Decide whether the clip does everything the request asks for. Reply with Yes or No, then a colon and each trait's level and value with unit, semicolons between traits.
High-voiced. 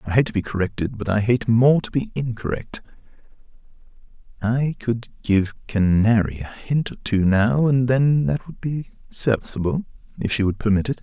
No: low, 115 Hz